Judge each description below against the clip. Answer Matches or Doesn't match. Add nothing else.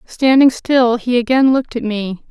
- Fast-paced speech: Doesn't match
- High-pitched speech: Matches